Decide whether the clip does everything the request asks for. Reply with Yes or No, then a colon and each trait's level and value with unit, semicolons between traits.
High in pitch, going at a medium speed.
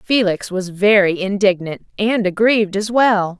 No: high, 200 Hz; slow, 125 wpm